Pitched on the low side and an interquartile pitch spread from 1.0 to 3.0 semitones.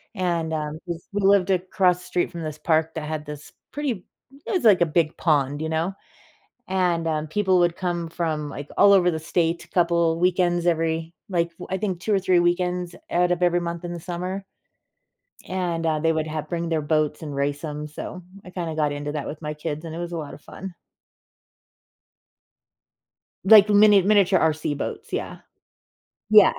No: medium, 170 Hz; narrow, 2.5 semitones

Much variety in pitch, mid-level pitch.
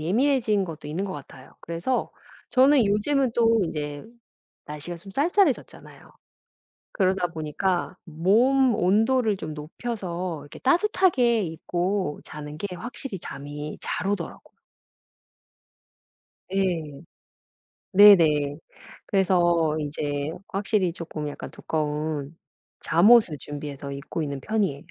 Yes: wide, 6.2 semitones; medium, 175 Hz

